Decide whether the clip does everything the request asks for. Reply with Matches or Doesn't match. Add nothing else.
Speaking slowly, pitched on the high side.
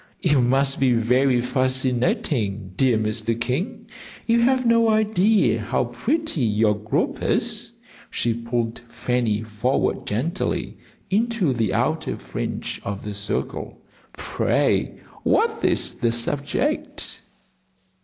Doesn't match